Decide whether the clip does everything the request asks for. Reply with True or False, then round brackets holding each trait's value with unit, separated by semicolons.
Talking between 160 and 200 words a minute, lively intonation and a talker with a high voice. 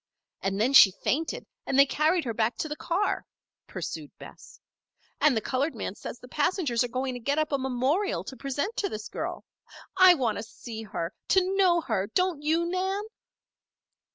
True (185 wpm; 6.7 semitones; 285 Hz)